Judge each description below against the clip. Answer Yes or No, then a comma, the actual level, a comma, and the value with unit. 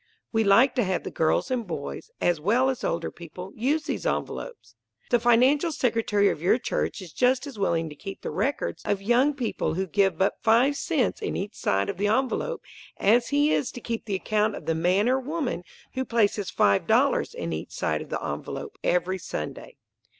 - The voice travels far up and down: Yes, wide, 5.7 semitones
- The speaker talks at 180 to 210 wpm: Yes, average, 200 wpm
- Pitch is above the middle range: Yes, high, 220 Hz